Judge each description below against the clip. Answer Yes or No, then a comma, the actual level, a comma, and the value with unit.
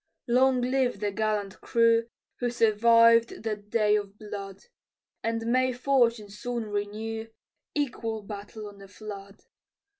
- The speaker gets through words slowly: Yes, slow, 125 wpm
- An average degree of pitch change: No, narrow, 2.3 semitones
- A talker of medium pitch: No, high, 225 Hz